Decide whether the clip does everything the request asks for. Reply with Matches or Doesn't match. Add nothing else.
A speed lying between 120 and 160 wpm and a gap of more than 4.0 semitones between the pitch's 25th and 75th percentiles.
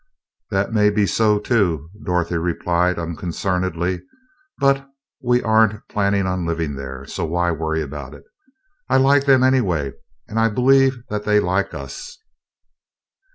Matches